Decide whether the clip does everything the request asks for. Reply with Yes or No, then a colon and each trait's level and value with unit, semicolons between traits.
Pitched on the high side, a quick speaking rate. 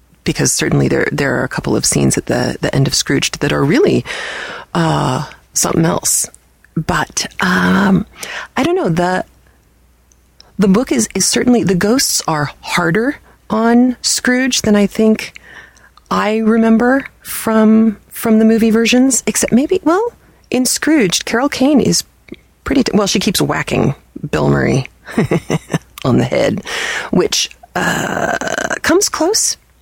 No: high, 220 Hz; average, 145 wpm